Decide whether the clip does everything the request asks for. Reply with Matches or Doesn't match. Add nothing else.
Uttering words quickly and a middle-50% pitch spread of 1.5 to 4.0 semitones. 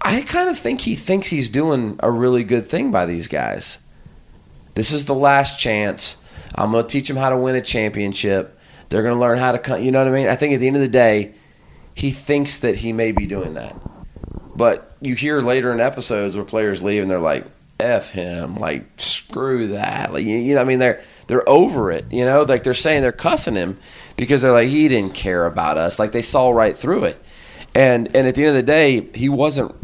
Doesn't match